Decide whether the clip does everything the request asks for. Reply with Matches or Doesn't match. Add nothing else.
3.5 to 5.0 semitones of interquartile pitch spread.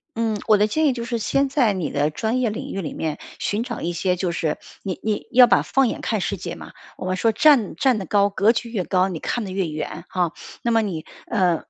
Matches